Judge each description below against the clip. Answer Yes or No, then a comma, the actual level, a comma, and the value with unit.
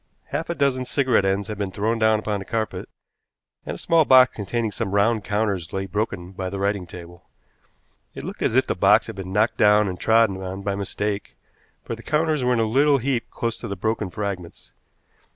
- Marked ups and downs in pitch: No, average, 3.2 semitones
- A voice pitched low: Yes, low, 105 Hz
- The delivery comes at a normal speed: No, fast, 210 wpm